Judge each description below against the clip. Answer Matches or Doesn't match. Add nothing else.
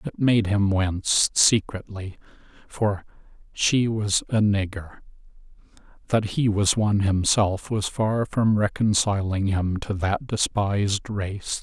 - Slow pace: Matches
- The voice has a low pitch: Matches